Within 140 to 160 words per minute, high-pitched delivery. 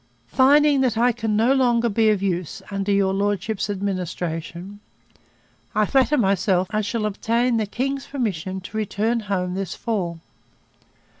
Yes: average, 145 wpm; high, 210 Hz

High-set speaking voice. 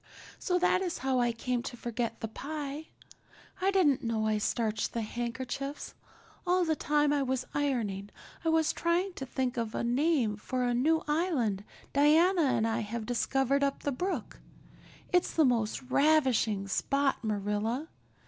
Yes: very high, 265 Hz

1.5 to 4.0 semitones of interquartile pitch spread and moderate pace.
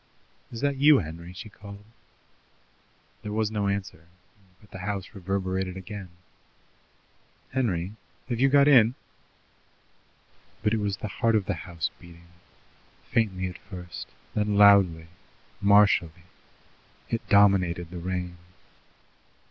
No: average, 3.0 semitones; slow, 120 wpm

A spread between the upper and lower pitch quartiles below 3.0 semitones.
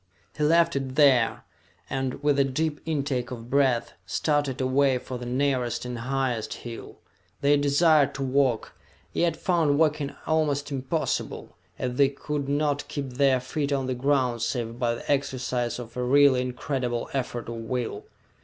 Yes: narrow, 2.6 semitones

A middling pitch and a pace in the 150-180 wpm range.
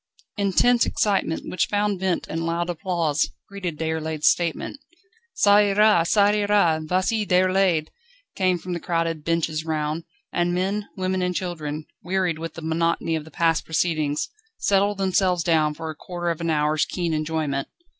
Yes: medium, 170 Hz; average, 160 wpm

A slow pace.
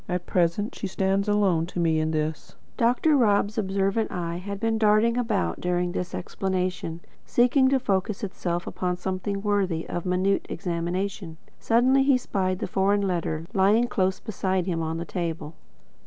No: average, 160 wpm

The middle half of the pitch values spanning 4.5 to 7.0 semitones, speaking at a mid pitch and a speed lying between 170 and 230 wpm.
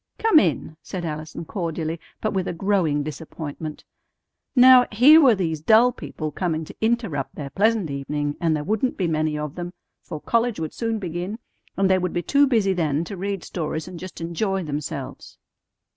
Yes: average, 5.2 semitones; medium, 175 Hz; average, 180 wpm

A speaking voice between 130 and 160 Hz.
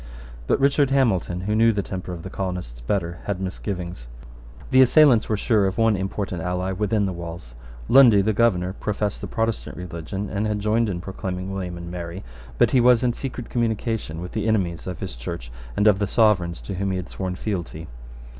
No: very low, 95 Hz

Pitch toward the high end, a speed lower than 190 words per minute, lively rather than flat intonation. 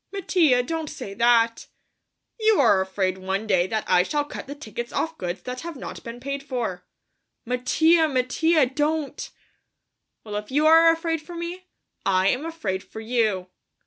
Yes: very high, 255 Hz; average, 165 wpm; wide, 7.3 semitones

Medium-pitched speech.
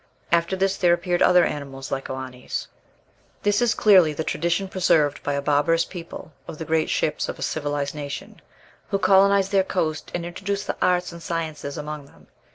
Yes: medium, 165 Hz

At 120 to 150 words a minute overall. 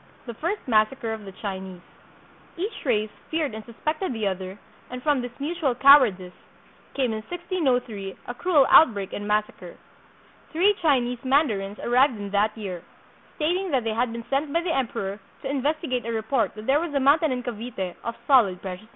No: average, 185 wpm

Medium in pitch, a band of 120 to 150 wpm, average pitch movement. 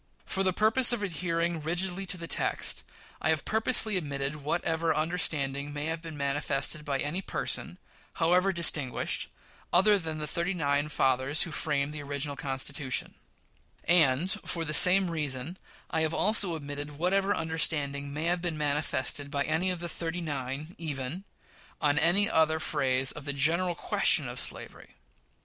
No: medium, 160 Hz; average, 160 wpm; average, 3.6 semitones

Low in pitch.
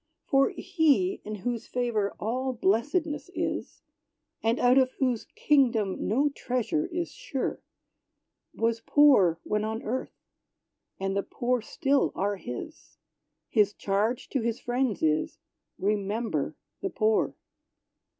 No: high, 240 Hz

